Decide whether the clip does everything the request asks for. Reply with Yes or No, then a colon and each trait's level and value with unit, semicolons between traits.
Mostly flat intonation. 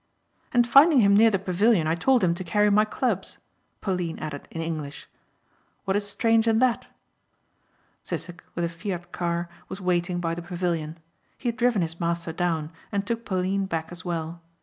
No: average, 3.9 semitones